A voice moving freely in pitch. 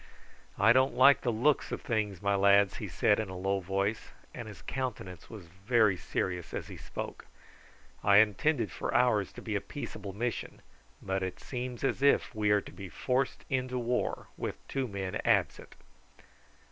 No: average, 4.3 semitones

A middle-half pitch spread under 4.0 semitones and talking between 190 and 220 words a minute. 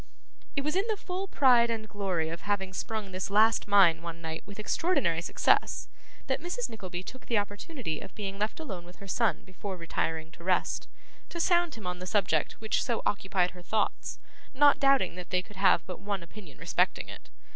No: average, 4.7 semitones; average, 200 wpm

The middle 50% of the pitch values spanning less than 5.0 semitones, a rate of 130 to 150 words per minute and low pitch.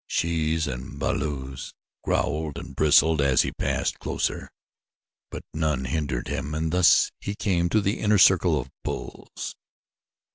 Yes: average, 3.5 semitones; average, 140 wpm; very low, 80 Hz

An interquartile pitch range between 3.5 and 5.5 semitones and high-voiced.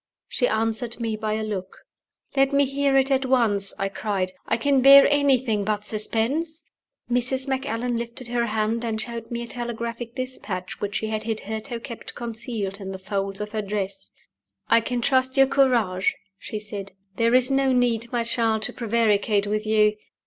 No: average, 3.0 semitones; high, 230 Hz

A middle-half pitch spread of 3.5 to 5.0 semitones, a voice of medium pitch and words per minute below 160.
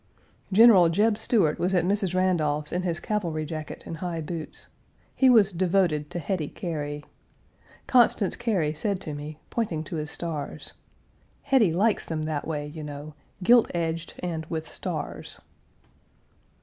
Yes: average, 4.1 semitones; medium, 170 Hz; average, 150 wpm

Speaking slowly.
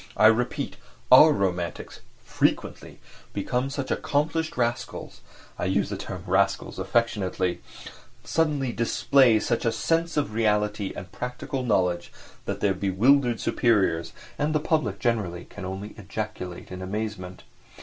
Yes: slow, 130 wpm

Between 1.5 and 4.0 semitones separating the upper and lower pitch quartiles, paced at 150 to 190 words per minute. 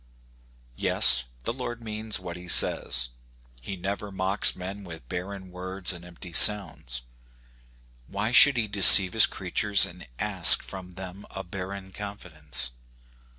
No: narrow, 2.5 semitones; slow, 135 wpm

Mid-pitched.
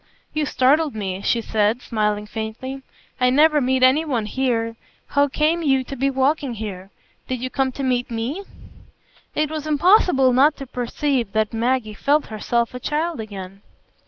No: very high, 255 Hz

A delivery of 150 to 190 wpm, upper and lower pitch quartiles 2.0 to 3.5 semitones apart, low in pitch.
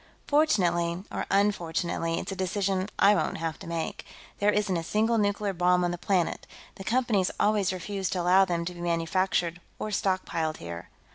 No: average, 180 wpm; average, 2.9 semitones; medium, 185 Hz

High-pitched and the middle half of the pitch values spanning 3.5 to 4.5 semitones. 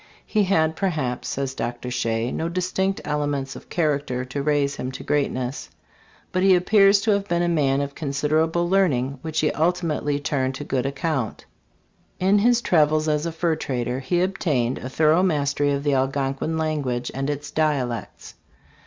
No: medium, 150 Hz; average, 4.1 semitones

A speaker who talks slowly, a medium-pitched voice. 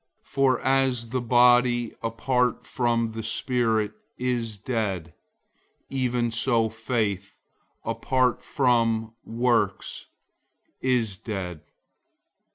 No: slow, 90 wpm; low, 115 Hz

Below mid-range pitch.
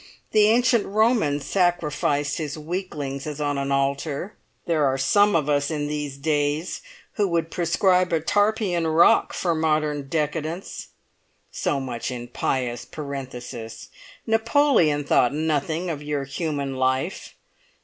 No: medium, 150 Hz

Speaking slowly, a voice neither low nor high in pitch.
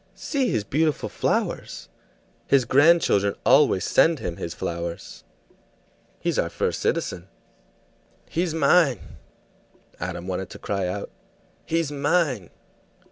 No: slow, 110 wpm; low, 125 Hz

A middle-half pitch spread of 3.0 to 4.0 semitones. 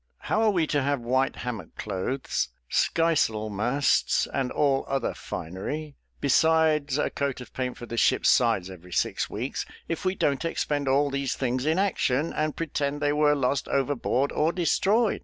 Yes: average, 3.5 semitones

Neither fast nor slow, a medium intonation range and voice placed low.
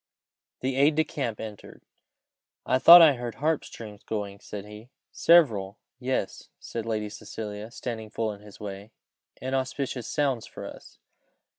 Yes: average, 145 wpm; average, 4.1 semitones; low, 115 Hz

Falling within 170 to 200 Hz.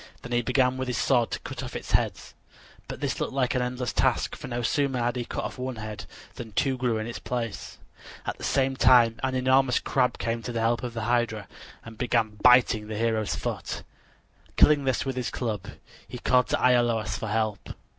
No: low, 120 Hz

